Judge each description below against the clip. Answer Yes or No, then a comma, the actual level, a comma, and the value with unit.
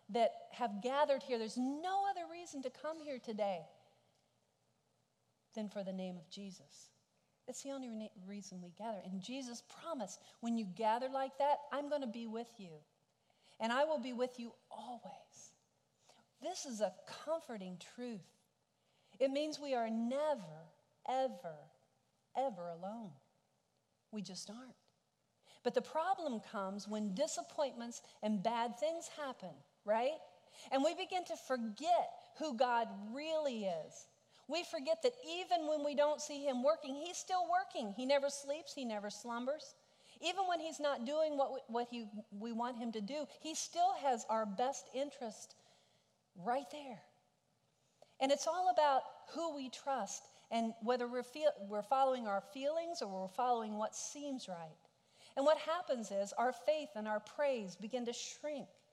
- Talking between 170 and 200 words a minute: No, average, 160 wpm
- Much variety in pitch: Yes, wide, 5.7 semitones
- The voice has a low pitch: No, very high, 255 Hz